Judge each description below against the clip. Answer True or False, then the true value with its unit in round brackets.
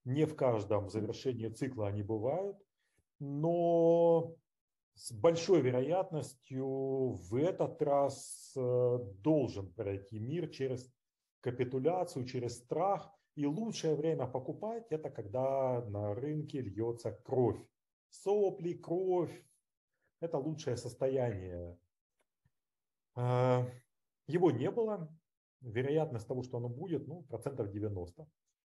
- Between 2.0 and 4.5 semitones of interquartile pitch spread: False (5.0 semitones)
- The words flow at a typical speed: False (100 wpm)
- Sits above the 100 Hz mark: True (130 Hz)